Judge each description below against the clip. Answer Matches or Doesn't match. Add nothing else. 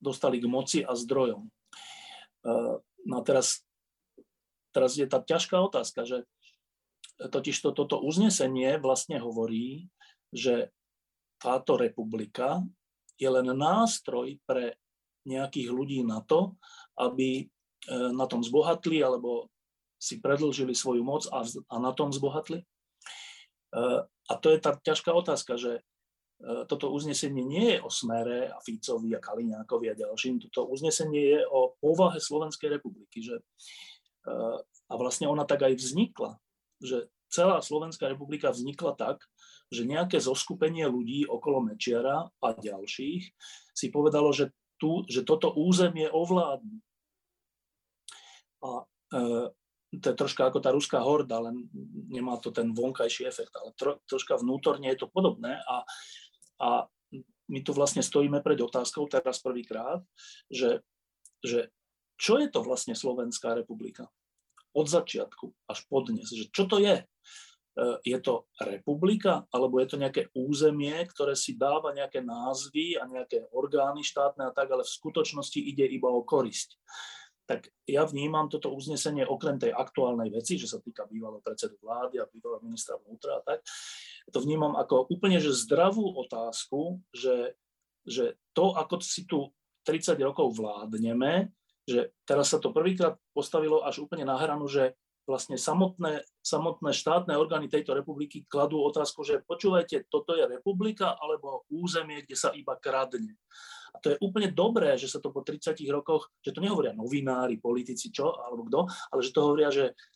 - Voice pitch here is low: Doesn't match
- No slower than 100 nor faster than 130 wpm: Doesn't match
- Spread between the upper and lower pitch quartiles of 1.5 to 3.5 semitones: Doesn't match